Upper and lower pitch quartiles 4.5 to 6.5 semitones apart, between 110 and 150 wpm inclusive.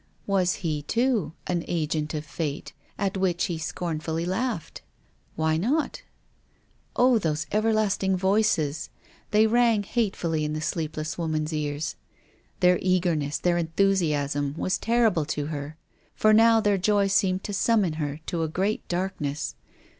Yes: average, 4.8 semitones; average, 145 wpm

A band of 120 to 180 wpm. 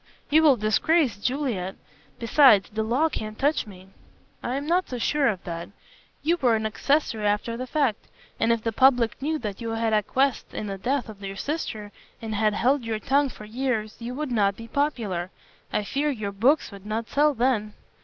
No: average, 195 wpm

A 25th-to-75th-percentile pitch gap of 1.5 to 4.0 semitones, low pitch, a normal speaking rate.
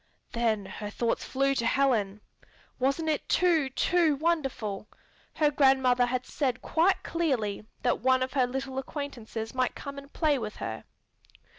No: average, 3.6 semitones; very high, 265 Hz; average, 150 wpm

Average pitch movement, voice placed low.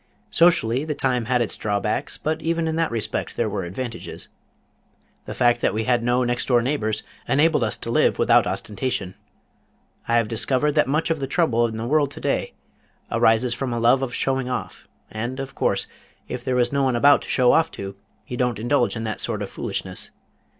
Yes: average, 3.1 semitones; low, 125 Hz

